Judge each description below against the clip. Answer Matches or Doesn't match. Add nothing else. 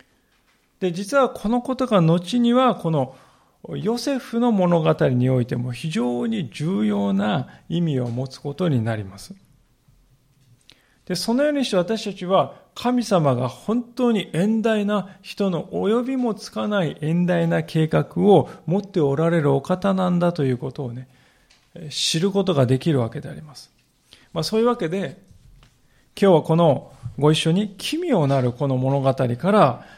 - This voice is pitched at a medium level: Matches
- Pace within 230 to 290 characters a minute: Matches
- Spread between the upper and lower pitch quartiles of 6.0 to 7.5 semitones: Matches